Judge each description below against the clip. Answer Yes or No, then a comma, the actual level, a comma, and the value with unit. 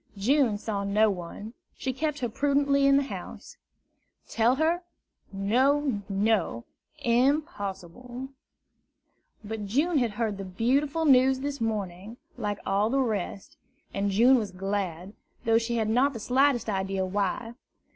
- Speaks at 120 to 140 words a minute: Yes, slow, 135 wpm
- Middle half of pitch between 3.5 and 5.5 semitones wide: Yes, average, 5.0 semitones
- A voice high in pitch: Yes, high, 225 Hz